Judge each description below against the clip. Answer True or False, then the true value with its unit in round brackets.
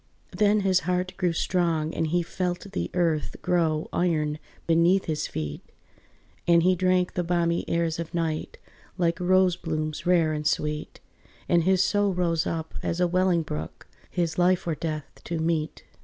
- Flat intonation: True (2.2 semitones)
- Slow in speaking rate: False (165 wpm)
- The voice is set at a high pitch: False (170 Hz)